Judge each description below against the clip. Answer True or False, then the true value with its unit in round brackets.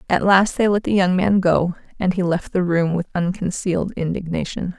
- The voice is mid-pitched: True (180 Hz)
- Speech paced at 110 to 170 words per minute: False (200 wpm)